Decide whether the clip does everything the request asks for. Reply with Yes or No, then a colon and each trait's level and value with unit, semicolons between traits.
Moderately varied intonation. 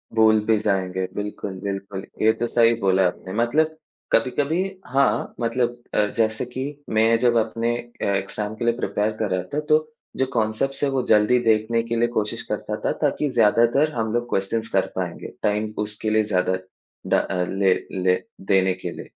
Yes: average, 3.1 semitones